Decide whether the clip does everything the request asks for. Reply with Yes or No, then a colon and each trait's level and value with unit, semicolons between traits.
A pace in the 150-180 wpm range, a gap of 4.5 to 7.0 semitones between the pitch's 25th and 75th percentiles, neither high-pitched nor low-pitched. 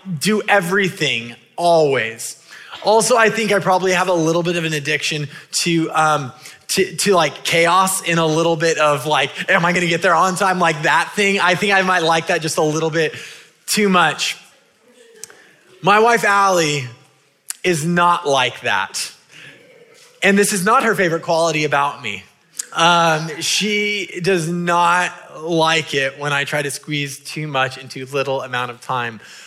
No: average, 170 wpm; average, 4.0 semitones; medium, 170 Hz